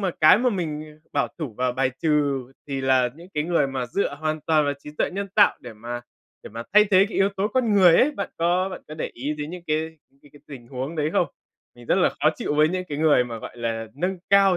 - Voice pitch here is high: No, medium, 155 Hz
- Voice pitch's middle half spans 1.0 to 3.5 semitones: No, wide, 5.4 semitones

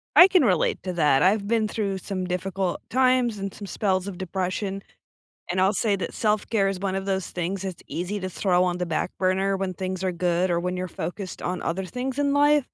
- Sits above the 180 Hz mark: Yes, high, 190 Hz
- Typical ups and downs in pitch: No, narrow, 2.2 semitones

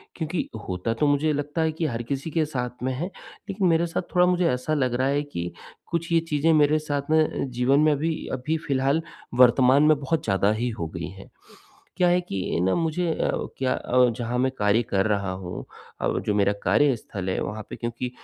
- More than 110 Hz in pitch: Yes, low, 135 Hz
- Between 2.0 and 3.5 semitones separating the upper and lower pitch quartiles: No, average, 5.2 semitones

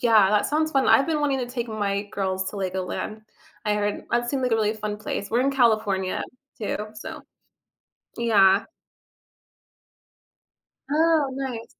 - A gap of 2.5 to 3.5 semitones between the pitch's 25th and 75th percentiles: No, average, 4.3 semitones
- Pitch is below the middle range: No, high, 220 Hz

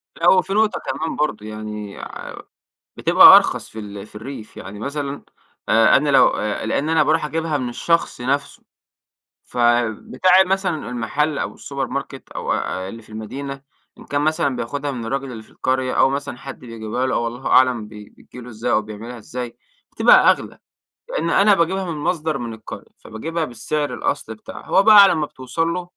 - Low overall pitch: Yes, low, 130 Hz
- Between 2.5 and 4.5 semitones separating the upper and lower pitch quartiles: No, average, 5.2 semitones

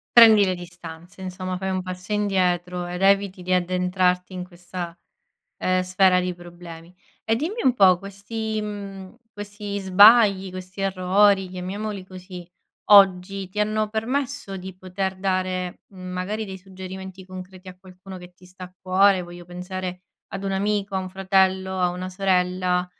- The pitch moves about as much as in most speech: No, narrow, 1.4 semitones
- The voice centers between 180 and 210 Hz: Yes, medium, 185 Hz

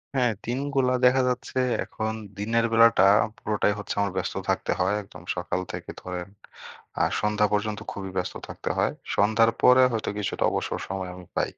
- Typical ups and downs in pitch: Yes, average, 3.4 semitones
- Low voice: Yes, low, 105 Hz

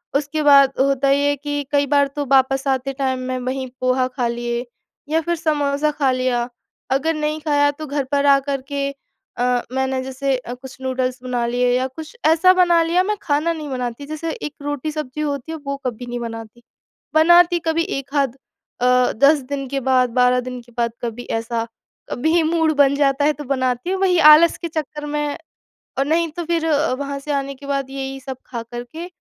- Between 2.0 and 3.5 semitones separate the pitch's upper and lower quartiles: Yes, average, 3.0 semitones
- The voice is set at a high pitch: Yes, very high, 280 Hz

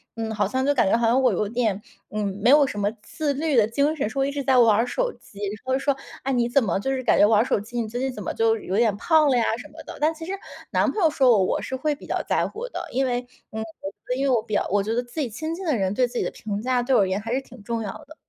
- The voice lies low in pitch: No, high, 245 Hz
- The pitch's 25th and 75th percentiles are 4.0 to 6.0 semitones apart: Yes, average, 4.4 semitones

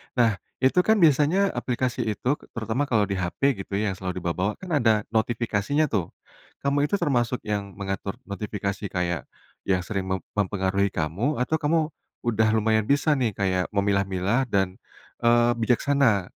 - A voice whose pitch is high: No, low, 110 Hz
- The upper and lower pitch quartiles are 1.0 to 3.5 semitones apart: No, average, 4.7 semitones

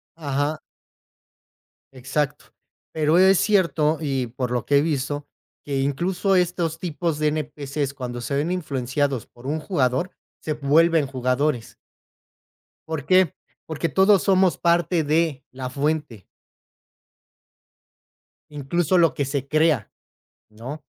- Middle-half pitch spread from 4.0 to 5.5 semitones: No, average, 3.6 semitones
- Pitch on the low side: No, medium, 150 Hz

